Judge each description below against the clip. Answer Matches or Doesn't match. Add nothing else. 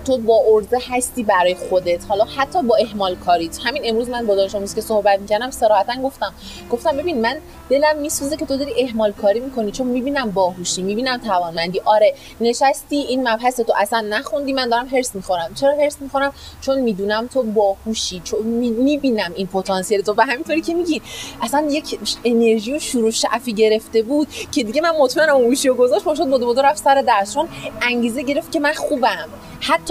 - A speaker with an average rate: Doesn't match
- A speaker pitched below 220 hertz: Doesn't match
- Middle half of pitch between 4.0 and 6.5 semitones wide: Matches